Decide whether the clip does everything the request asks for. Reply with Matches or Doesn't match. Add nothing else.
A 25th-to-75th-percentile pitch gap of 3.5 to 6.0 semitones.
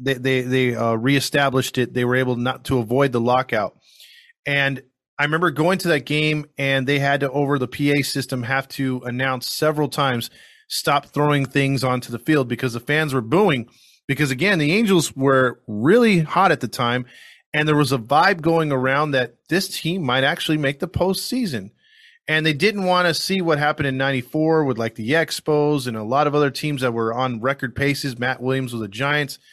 Doesn't match